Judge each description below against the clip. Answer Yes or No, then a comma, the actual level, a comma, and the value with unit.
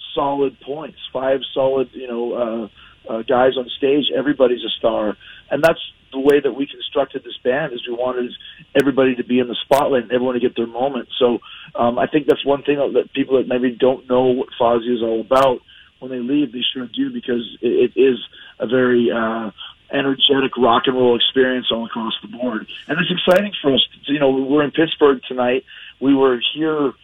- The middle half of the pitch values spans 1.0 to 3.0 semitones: Yes, narrow, 2.4 semitones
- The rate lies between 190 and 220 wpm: Yes, fast, 205 wpm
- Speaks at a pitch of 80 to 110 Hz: No, low, 130 Hz